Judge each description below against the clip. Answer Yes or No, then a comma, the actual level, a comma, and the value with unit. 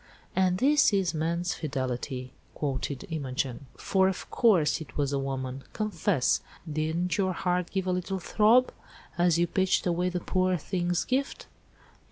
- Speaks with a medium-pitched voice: Yes, medium, 175 Hz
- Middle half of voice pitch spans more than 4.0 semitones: Yes, average, 4.6 semitones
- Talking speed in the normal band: Yes, average, 150 wpm